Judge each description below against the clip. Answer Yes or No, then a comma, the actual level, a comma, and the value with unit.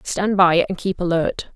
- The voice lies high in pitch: No, medium, 180 Hz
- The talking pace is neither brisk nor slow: Yes, average, 195 wpm